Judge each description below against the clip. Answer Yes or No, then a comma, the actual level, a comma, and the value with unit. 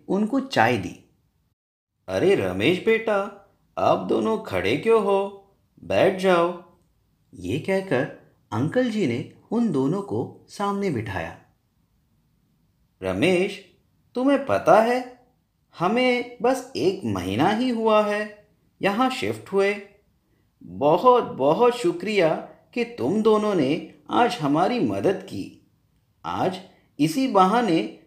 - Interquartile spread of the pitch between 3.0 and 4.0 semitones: No, average, 4.4 semitones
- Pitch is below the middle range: No, high, 210 Hz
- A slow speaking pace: Yes, slow, 110 wpm